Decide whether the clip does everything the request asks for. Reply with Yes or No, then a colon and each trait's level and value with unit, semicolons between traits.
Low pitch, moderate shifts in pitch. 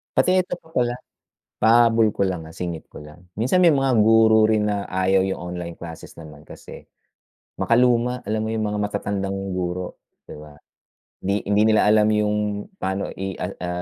Yes: low, 105 Hz; average, 3.4 semitones